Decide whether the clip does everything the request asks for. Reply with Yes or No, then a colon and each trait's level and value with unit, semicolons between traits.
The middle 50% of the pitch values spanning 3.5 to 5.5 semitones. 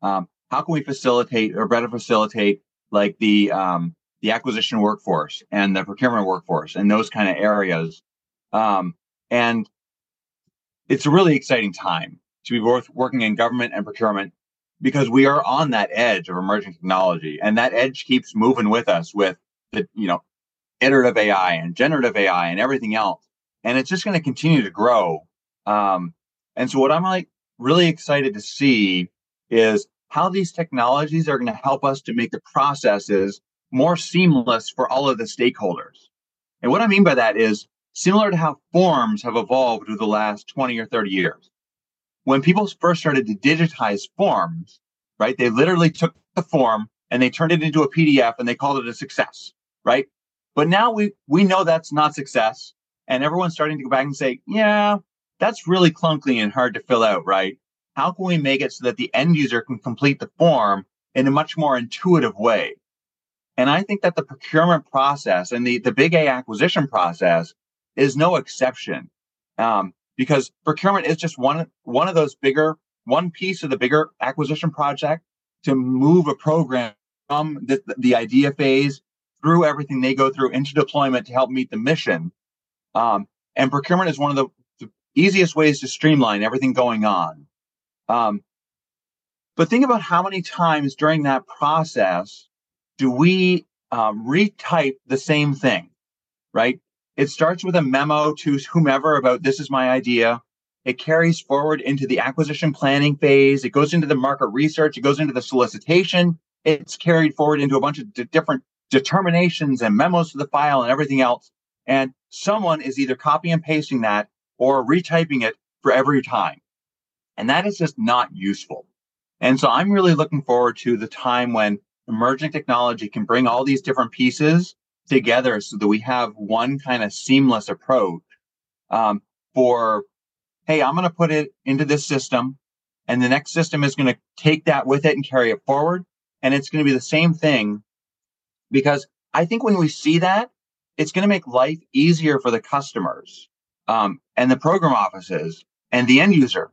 Yes: average, 4.6 semitones